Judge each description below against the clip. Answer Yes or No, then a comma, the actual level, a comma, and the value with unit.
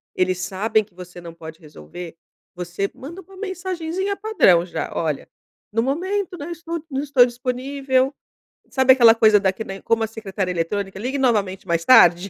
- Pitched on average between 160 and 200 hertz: No, high, 225 Hz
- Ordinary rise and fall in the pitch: No, wide, 7.5 semitones